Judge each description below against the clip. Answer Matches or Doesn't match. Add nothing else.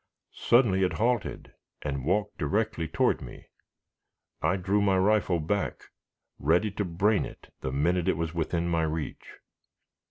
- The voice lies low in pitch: Matches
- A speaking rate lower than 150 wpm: Matches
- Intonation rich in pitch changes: Doesn't match